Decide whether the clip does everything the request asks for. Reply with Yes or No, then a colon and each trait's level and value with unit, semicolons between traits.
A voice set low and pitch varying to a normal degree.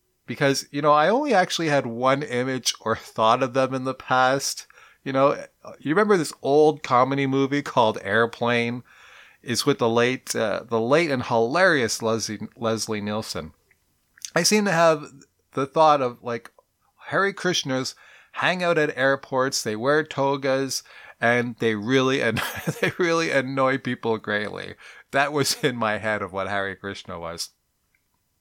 Yes: low, 130 Hz; average, 3.9 semitones